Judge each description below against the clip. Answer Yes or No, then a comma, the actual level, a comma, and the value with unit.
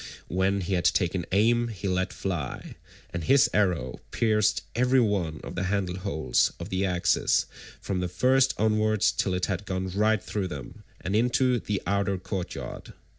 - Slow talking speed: No, average, 170 wpm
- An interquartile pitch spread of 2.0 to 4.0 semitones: Yes, average, 3.0 semitones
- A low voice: Yes, very low, 95 Hz